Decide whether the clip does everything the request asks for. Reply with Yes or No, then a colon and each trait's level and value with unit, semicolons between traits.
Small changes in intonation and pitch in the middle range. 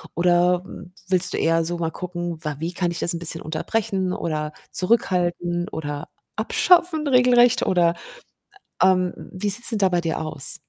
Yes: narrow, 2.2 semitones; medium, 175 Hz